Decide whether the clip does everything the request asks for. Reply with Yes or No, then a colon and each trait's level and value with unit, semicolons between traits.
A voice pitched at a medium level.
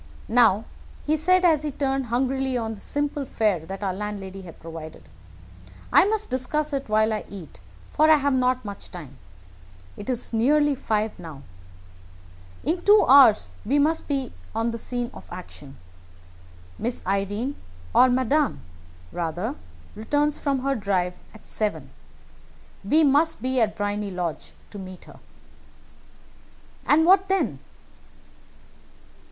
No: high, 240 Hz